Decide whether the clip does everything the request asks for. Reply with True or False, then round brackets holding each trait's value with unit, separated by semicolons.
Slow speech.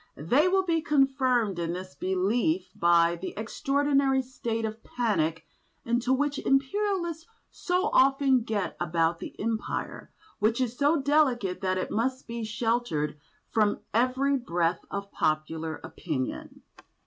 True (130 wpm)